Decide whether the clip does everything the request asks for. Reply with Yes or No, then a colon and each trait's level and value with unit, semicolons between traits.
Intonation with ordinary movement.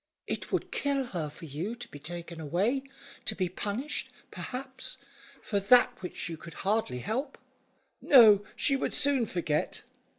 No: wide, 6.8 semitones